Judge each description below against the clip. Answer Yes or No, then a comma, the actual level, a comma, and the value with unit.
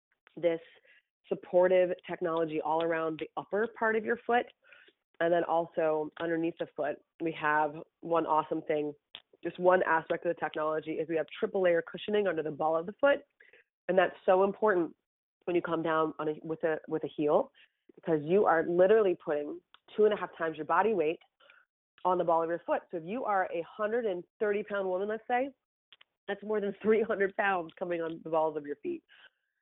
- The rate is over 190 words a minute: Yes, average, 200 wpm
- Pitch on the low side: No, medium, 175 Hz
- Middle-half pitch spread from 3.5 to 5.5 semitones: Yes, average, 4.7 semitones